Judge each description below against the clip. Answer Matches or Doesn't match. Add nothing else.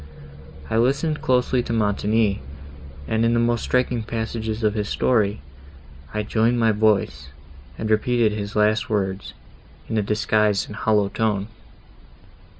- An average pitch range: Doesn't match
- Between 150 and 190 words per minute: Doesn't match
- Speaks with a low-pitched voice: Matches